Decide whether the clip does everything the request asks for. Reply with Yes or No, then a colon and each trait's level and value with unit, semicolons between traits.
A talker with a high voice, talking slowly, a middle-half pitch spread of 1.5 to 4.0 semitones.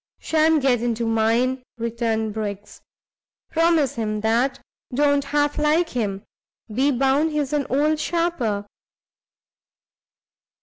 No: very high, 260 Hz; slow, 105 wpm; average, 4.8 semitones